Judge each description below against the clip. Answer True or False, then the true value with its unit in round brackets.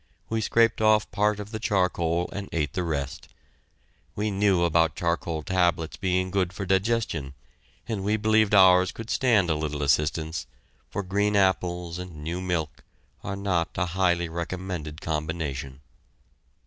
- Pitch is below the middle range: True (90 Hz)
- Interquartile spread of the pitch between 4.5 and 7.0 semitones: False (3.5 semitones)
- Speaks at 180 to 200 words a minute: False (150 wpm)